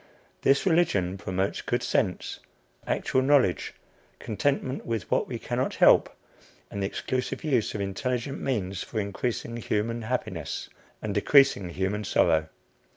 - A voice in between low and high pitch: No, low, 115 Hz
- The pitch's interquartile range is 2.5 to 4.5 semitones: No, average, 5.1 semitones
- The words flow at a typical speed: No, slow, 130 wpm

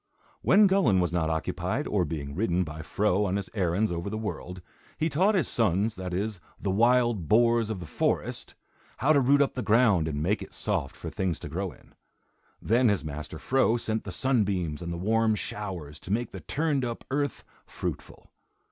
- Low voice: Yes, low, 105 Hz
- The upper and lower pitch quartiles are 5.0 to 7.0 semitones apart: Yes, average, 5.3 semitones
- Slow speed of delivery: No, average, 195 wpm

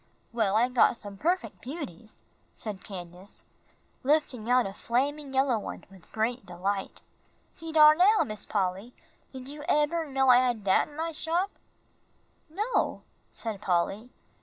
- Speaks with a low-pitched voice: No, high, 245 Hz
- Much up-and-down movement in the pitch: Yes, wide, 6.8 semitones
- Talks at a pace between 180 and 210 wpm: No, average, 145 wpm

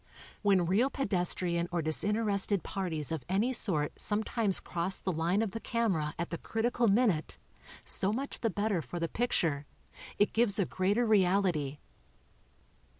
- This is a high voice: Yes, high, 195 Hz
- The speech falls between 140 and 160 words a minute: Yes, average, 155 wpm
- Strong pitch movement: No, average, 4.4 semitones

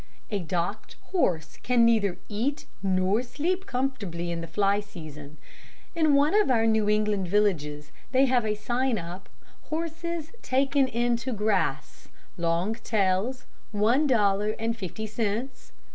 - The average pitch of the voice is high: Yes, high, 215 Hz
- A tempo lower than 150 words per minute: Yes, average, 140 wpm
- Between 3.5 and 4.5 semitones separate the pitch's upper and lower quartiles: No, wide, 5.4 semitones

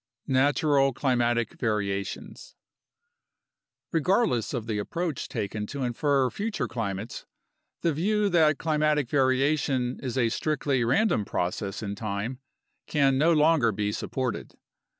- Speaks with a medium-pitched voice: No, low, 130 Hz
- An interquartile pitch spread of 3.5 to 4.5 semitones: No, average, 5.2 semitones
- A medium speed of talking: No, slow, 115 wpm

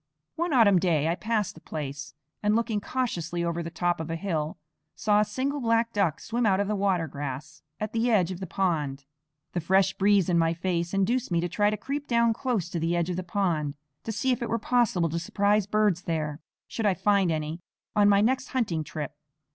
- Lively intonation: No, average, 4.5 semitones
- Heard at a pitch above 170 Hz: Yes, high, 190 Hz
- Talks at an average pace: No, fast, 220 wpm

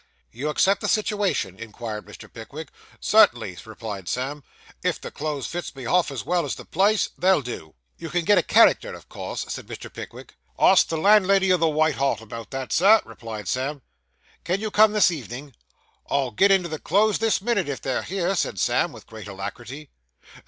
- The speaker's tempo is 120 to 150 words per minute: No, average, 190 wpm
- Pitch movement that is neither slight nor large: No, wide, 7.8 semitones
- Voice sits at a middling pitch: Yes, medium, 155 Hz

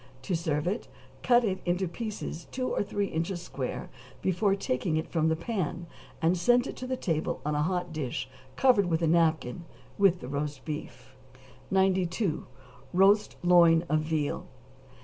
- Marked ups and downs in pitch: No, average, 3.7 semitones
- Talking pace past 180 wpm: No, average, 165 wpm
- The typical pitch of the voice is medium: Yes, medium, 175 Hz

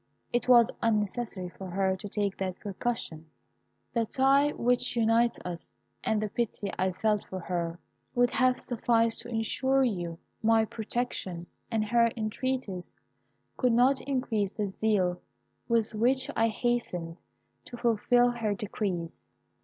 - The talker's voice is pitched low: No, high, 220 Hz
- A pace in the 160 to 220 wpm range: No, average, 140 wpm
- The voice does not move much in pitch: No, average, 4.0 semitones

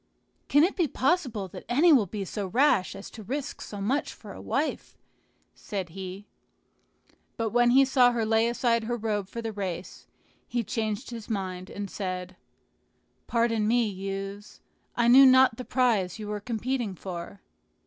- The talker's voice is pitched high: Yes, high, 220 Hz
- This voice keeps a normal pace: Yes, average, 170 wpm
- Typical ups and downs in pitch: Yes, average, 3.9 semitones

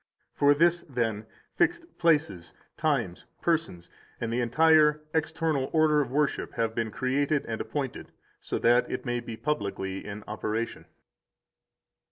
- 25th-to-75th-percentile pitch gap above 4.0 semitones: Yes, wide, 5.5 semitones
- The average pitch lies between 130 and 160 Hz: Yes, low, 135 Hz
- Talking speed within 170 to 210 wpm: No, slow, 135 wpm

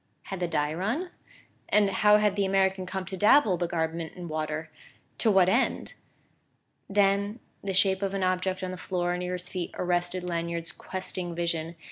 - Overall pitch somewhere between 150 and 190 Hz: Yes, medium, 185 Hz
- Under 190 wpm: Yes, average, 175 wpm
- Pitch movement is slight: Yes, narrow, 2.2 semitones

